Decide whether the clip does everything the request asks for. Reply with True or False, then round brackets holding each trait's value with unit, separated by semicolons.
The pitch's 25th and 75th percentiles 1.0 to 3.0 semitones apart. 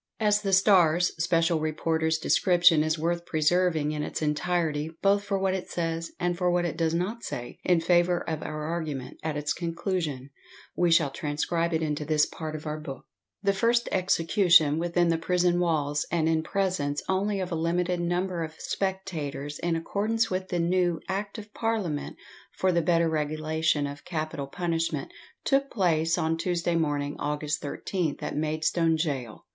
True (2.6 semitones)